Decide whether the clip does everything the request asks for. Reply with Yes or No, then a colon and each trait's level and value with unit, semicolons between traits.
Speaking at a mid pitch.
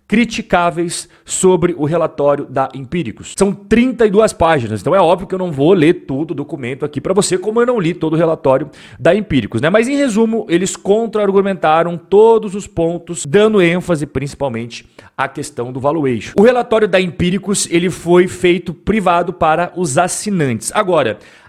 Yes: medium, 175 Hz